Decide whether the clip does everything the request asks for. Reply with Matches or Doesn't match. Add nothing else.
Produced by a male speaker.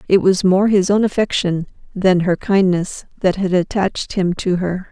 Doesn't match